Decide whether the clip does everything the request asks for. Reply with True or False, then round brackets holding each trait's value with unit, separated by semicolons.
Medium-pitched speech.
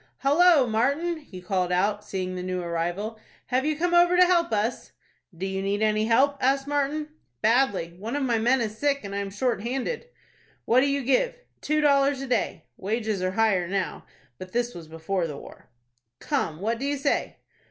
False (230 Hz)